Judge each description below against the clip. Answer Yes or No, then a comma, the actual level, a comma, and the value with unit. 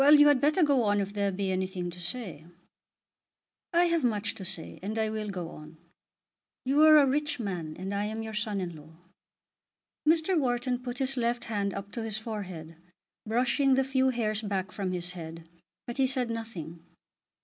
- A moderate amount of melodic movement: No, wide, 5.7 semitones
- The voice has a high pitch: Yes, high, 215 Hz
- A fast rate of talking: No, average, 190 wpm